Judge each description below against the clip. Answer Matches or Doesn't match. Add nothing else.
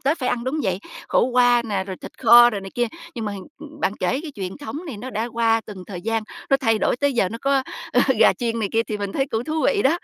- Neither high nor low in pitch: Doesn't match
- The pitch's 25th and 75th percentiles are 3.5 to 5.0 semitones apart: Matches